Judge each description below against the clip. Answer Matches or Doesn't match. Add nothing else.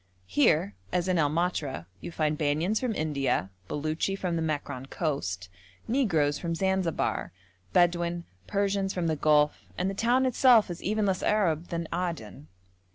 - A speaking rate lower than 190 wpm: Matches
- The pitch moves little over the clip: Doesn't match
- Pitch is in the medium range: Matches